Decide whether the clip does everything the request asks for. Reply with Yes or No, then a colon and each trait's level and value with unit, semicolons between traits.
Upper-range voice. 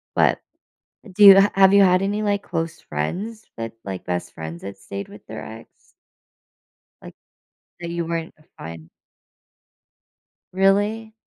No: medium, 175 Hz